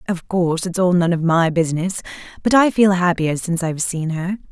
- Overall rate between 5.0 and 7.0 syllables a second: Yes, 5.8 syllables/s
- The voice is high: No, medium, 175 Hz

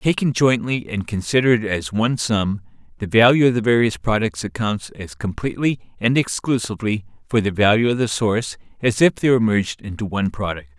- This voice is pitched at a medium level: No, low, 110 Hz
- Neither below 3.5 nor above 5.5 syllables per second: No, 5.8 syllables/s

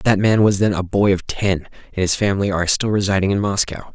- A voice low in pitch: Yes, low, 100 Hz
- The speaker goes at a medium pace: No, fast, 245 wpm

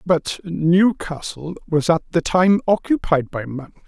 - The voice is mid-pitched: Yes, medium, 170 Hz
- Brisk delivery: No, average, 140 wpm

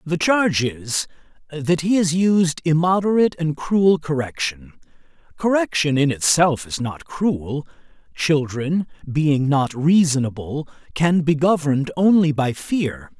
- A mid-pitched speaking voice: Yes, medium, 155 Hz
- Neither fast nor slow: No, slow, 125 wpm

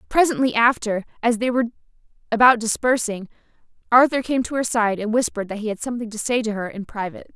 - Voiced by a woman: Yes, female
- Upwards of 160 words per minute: Yes, average, 195 wpm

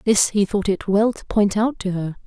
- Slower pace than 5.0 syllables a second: Yes, 4.8 syllables/s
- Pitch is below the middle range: No, high, 205 Hz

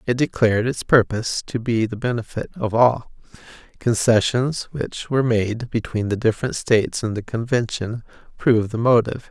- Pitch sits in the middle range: No, low, 115 Hz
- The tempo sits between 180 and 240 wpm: No, average, 155 wpm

